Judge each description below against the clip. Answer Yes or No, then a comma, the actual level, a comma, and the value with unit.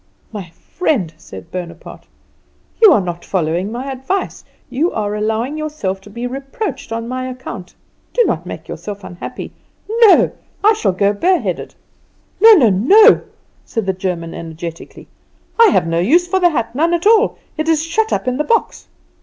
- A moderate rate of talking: Yes, average, 170 wpm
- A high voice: Yes, high, 245 Hz